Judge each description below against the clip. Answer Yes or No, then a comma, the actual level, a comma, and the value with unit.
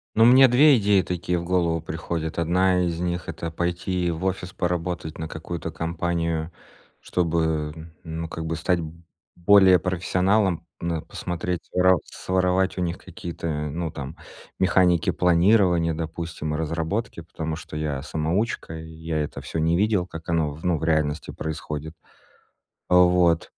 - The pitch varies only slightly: Yes, narrow, 2.0 semitones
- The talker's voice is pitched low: Yes, very low, 85 Hz